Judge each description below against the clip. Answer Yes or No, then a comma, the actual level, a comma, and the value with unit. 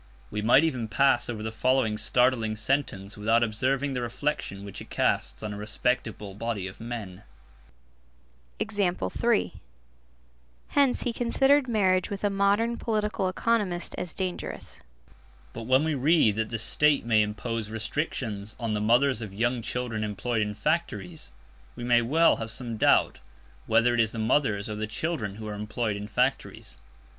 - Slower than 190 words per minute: Yes, average, 155 wpm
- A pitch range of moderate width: No, wide, 6.1 semitones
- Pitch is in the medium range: No, low, 120 Hz